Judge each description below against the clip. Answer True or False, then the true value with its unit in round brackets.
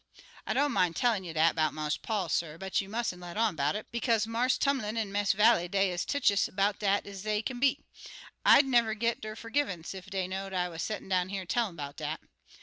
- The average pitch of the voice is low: False (200 Hz)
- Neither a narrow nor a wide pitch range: True (4.2 semitones)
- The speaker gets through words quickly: True (230 wpm)